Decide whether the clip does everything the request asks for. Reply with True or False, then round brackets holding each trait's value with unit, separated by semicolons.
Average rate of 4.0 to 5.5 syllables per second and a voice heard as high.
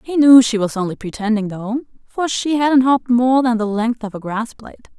True (5.4 syllables/s; 235 Hz)